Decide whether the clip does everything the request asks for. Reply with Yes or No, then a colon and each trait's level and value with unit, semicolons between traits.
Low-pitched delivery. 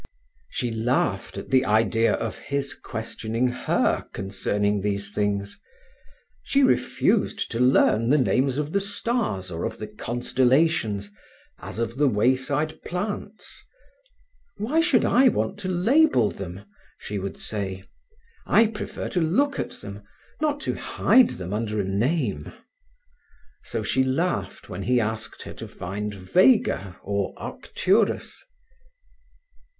Yes: low, 120 Hz